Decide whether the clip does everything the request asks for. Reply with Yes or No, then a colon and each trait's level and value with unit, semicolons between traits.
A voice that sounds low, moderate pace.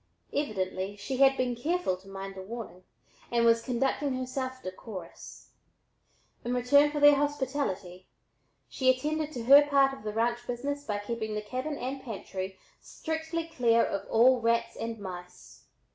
No: high, 240 Hz; average, 155 wpm